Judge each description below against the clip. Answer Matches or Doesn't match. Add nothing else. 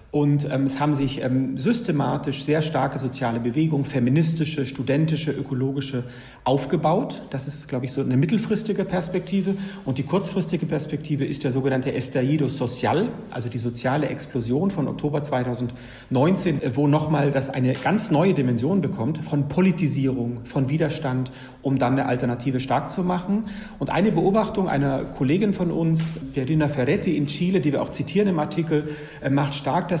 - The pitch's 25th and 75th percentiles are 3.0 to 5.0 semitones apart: Matches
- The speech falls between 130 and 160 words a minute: Matches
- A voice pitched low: Doesn't match